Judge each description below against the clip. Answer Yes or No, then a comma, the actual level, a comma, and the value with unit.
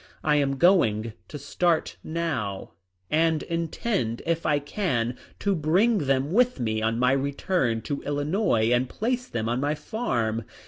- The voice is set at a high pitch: No, medium, 145 Hz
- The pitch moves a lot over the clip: Yes, wide, 6.3 semitones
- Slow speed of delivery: No, average, 150 wpm